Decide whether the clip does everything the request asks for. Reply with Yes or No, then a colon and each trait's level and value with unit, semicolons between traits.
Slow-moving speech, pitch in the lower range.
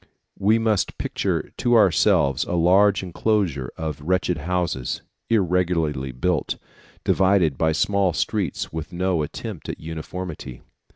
Yes: slow, 120 wpm; very low, 90 Hz